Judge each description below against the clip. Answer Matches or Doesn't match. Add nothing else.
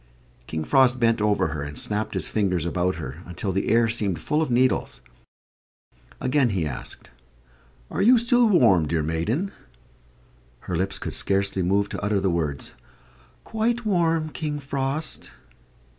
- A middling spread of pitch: Doesn't match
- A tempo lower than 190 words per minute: Matches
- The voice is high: Doesn't match